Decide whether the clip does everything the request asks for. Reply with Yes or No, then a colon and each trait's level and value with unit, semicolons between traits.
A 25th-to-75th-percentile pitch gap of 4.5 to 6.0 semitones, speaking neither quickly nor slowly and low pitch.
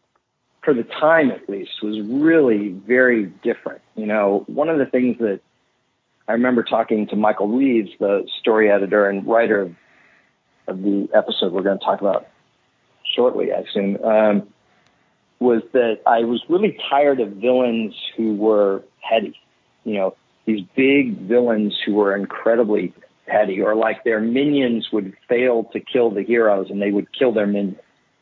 No: average, 3.1 semitones; average, 160 wpm; low, 110 Hz